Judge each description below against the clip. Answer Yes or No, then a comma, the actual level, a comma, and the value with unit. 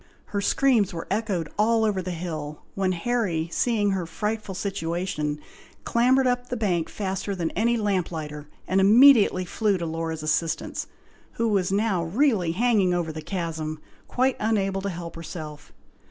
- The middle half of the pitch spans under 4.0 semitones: No, average, 4.7 semitones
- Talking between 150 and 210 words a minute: Yes, average, 155 wpm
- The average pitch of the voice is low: No, high, 190 Hz